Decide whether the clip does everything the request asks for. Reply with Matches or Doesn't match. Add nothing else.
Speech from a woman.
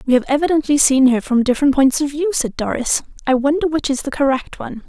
Matches